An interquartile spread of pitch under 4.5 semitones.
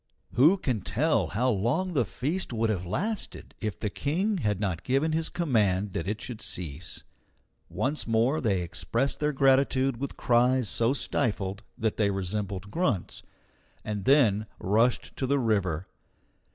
No: wide, 5.4 semitones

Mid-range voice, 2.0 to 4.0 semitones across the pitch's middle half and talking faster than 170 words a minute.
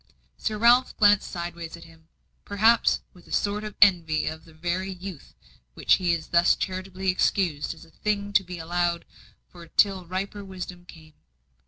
No: medium, 180 Hz; average, 2.9 semitones; average, 165 wpm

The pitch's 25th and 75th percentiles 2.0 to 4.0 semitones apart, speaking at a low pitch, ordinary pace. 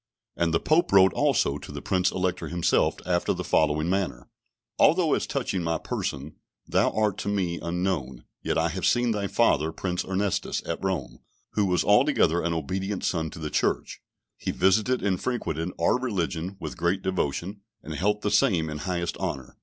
Yes: average, 3.3 semitones; very low, 90 Hz; average, 180 wpm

